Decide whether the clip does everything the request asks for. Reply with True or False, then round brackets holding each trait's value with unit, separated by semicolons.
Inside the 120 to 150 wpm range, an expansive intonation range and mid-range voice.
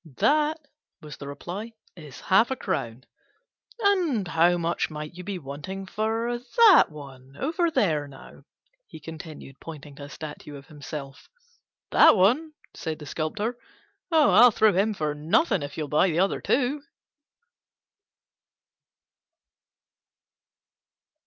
True (135 wpm; 7.5 semitones; 175 Hz)